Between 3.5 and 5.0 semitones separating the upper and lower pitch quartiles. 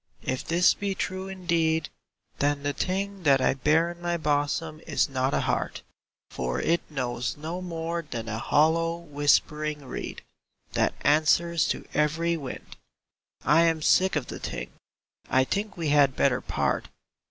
No: average, 3.0 semitones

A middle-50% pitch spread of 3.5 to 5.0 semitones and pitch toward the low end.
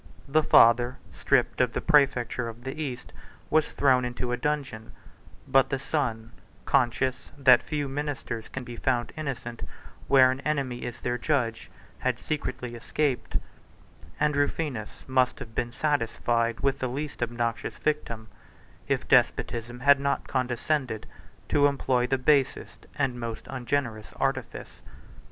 No: average, 3.0 semitones; low, 130 Hz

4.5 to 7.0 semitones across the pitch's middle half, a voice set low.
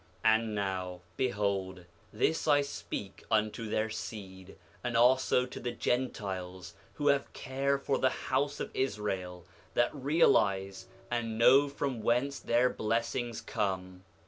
Yes: average, 5.1 semitones; low, 115 Hz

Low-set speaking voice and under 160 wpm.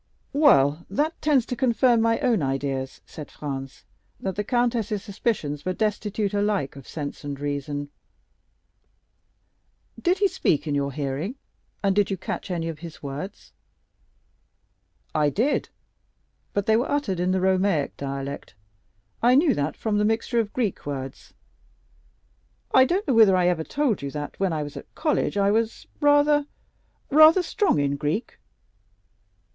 No: high, 195 Hz; average, 150 wpm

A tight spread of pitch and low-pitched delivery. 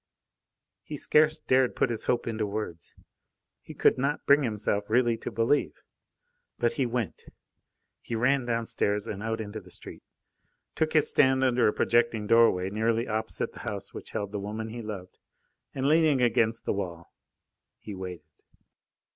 No: average, 3.3 semitones; low, 115 Hz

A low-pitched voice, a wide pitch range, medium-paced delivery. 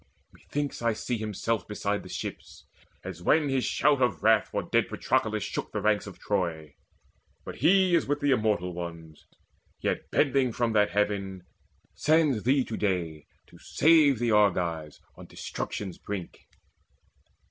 Yes: low, 105 Hz; wide, 6.6 semitones; average, 150 wpm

